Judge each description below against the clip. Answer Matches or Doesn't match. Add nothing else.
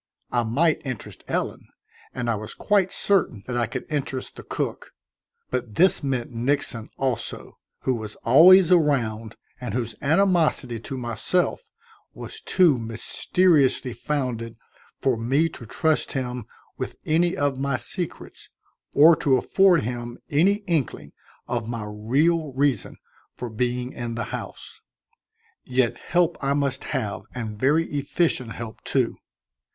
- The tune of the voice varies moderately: Matches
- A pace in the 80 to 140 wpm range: Matches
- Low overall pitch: Matches